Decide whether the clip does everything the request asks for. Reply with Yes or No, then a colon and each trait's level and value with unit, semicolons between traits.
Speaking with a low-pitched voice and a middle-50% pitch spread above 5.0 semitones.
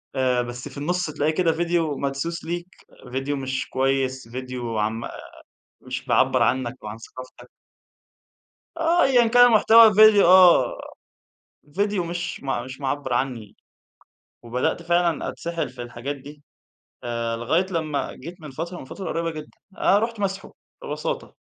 No: medium, 145 Hz; wide, 5.6 semitones